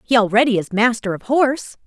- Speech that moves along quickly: No, average, 195 wpm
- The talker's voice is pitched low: No, high, 230 Hz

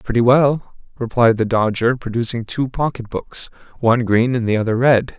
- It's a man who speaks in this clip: Yes, male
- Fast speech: No, average, 175 wpm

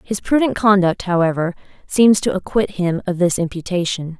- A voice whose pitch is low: No, medium, 185 Hz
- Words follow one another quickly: No, average, 155 wpm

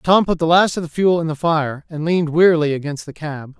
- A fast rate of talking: Yes, fast, 265 wpm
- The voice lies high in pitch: No, medium, 160 Hz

